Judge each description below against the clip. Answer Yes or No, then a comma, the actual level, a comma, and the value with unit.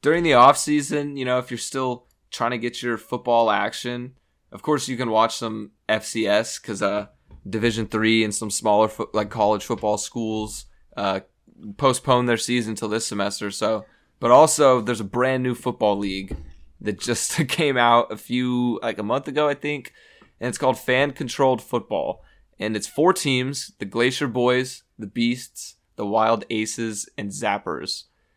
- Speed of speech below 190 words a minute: Yes, average, 175 wpm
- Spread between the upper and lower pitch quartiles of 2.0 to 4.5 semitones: Yes, average, 2.9 semitones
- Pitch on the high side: No, low, 120 Hz